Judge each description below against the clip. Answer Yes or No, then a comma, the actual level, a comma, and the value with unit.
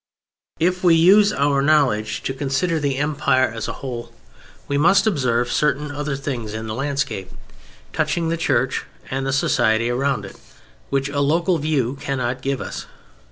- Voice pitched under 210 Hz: Yes, medium, 140 Hz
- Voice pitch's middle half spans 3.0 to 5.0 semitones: Yes, average, 3.5 semitones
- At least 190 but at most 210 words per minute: No, average, 160 wpm